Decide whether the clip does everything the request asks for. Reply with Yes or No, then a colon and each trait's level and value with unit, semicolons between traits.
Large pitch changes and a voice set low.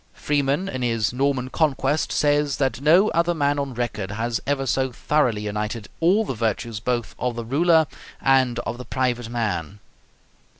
No: average, 3.8 semitones; low, 130 Hz